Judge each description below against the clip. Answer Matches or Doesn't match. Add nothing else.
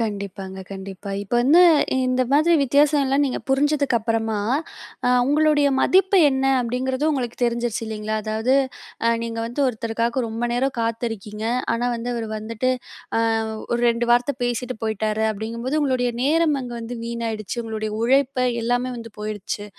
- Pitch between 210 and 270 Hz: Matches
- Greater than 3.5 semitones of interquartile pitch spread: Doesn't match